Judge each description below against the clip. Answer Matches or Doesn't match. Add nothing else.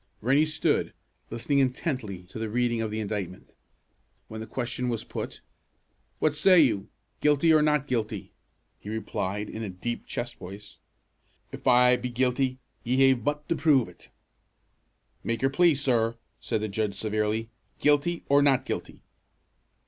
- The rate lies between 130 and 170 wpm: Matches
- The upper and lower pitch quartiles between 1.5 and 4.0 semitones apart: Doesn't match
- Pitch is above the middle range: Doesn't match